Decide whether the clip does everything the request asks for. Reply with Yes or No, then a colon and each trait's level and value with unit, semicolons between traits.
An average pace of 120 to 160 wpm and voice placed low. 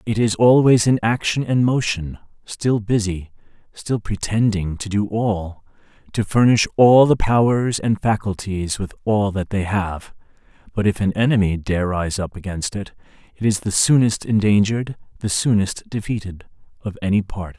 Yes: average, 155 wpm; low, 105 Hz